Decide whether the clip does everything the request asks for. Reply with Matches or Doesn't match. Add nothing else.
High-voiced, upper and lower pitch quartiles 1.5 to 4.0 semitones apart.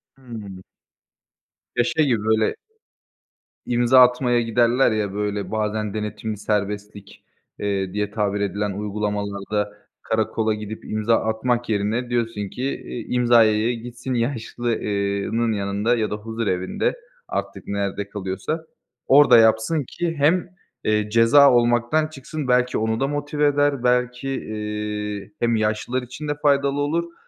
Doesn't match